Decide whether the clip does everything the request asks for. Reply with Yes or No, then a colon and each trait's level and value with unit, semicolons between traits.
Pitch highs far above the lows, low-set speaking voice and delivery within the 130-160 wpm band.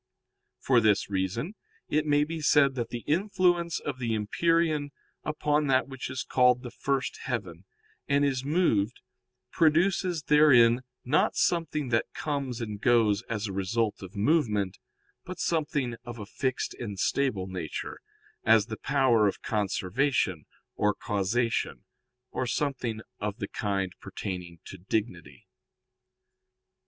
Yes: wide, 6.0 semitones; low, 120 Hz; slow, 135 wpm